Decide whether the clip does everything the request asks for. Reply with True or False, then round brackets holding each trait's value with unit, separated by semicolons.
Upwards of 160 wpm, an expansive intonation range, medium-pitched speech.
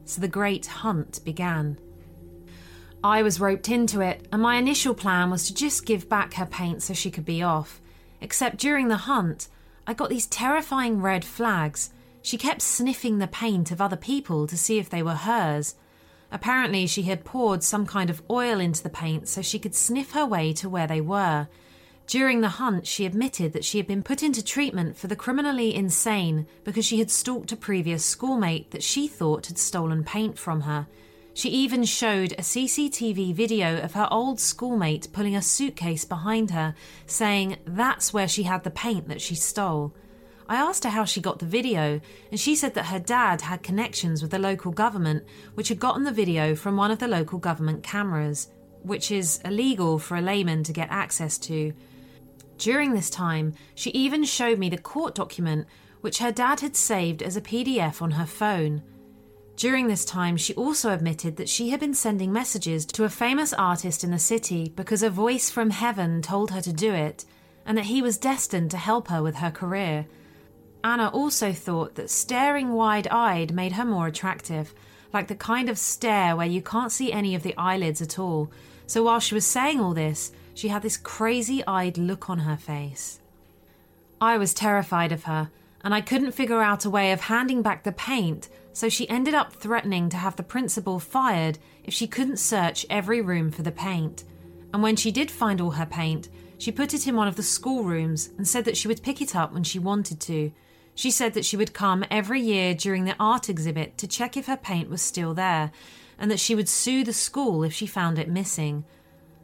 False (200 wpm; 5.7 semitones; 195 Hz)